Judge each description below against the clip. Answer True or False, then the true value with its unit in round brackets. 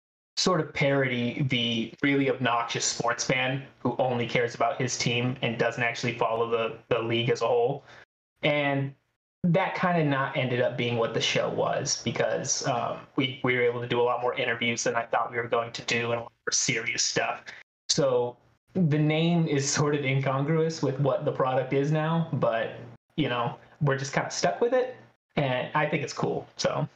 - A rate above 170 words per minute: True (205 wpm)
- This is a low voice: True (130 Hz)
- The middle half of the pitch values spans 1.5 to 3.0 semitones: False (3.5 semitones)